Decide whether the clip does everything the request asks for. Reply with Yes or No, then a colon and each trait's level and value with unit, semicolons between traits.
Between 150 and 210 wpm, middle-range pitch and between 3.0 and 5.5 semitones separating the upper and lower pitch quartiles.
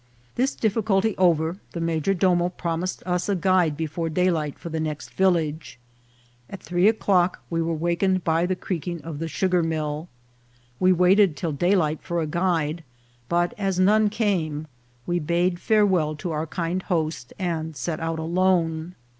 No: average, 160 wpm; medium, 175 Hz; narrow, 2.5 semitones